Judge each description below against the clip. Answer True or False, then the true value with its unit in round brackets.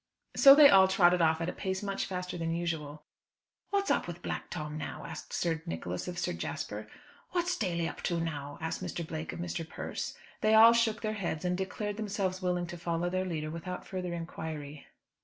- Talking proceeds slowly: False (200 wpm)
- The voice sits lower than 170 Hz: False (175 Hz)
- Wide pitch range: False (3.0 semitones)